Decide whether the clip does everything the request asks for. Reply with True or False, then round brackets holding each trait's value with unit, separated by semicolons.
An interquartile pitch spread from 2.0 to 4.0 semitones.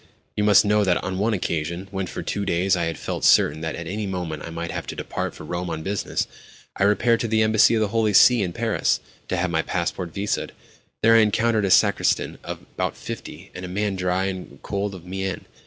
True (3.2 semitones)